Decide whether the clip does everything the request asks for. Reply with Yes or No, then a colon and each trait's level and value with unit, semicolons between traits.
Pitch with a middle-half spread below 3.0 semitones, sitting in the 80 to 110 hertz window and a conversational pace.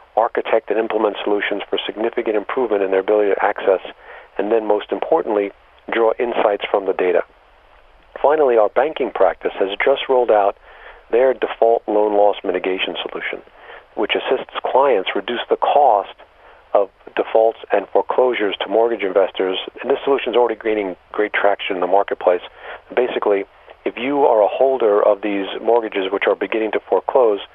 Yes: narrow, 2.4 semitones; low, 105 Hz; average, 160 wpm